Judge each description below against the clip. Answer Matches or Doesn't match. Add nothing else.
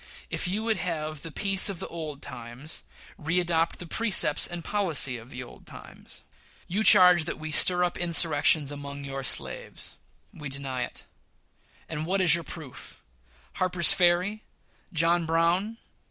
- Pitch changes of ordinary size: Matches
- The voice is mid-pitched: Matches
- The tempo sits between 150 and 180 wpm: Matches